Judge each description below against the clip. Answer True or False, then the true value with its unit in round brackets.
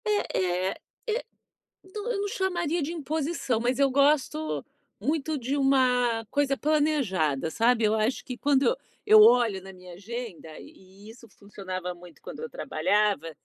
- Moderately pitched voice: False (250 Hz)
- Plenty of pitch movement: True (7.8 semitones)